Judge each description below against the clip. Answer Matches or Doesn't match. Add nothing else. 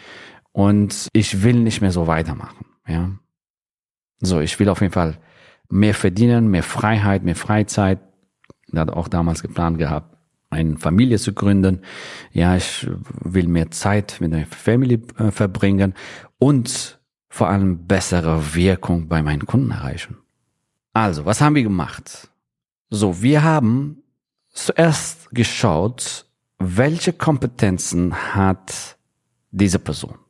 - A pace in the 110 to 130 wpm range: Matches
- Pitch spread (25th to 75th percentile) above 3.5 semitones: Matches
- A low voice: Matches